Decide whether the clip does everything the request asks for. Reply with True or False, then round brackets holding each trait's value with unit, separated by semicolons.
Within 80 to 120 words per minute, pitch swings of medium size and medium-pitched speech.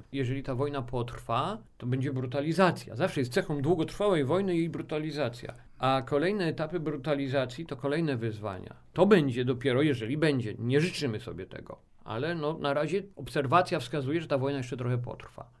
False (160 wpm; 3.6 semitones; 145 Hz)